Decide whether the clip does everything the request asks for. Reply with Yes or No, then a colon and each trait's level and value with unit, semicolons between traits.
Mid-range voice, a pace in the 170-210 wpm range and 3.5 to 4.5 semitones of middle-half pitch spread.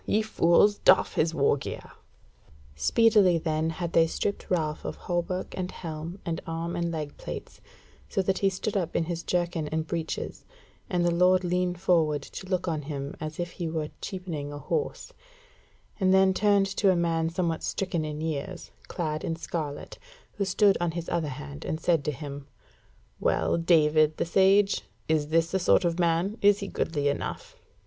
No: medium, 170 Hz; average, 180 wpm; average, 3.0 semitones